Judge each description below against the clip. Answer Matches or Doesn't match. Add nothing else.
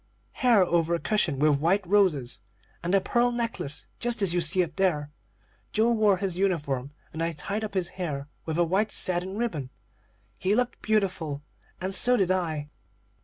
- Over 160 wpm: Matches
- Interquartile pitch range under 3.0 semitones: Doesn't match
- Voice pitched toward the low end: Doesn't match